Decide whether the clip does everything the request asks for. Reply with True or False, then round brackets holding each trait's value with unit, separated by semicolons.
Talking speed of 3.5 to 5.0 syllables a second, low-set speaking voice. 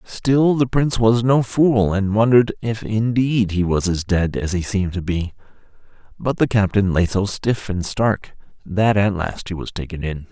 True (4.6 syllables/s; 105 Hz)